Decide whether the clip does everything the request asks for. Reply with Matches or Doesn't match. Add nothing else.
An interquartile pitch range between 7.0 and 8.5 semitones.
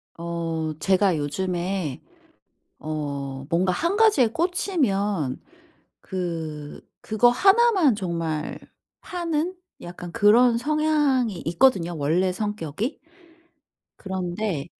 Matches